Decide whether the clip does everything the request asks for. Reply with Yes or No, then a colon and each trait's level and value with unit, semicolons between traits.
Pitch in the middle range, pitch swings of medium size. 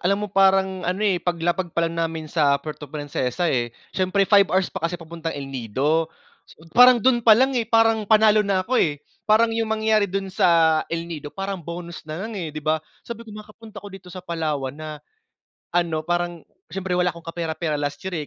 Yes: medium, 175 Hz; average, 4.1 semitones